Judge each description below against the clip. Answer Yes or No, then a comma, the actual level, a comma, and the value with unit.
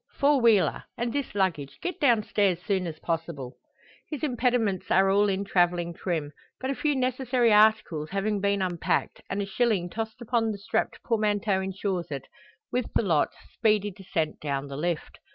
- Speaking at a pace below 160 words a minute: No, average, 170 wpm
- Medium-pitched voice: No, high, 200 Hz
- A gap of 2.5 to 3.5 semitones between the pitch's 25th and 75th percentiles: No, average, 4.7 semitones